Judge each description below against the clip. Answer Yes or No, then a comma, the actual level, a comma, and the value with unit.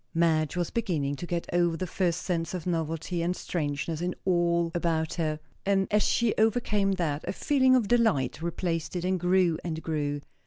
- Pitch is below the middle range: No, medium, 175 Hz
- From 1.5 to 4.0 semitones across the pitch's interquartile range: Yes, average, 2.7 semitones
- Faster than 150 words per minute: Yes, average, 185 wpm